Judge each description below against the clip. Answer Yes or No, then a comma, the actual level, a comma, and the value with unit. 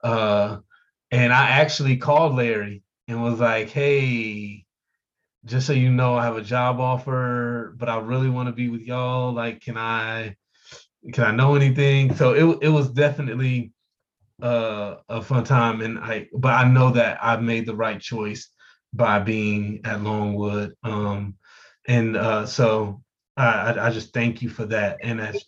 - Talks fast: No, average, 165 wpm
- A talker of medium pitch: No, low, 120 Hz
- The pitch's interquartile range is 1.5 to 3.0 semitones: Yes, narrow, 2.4 semitones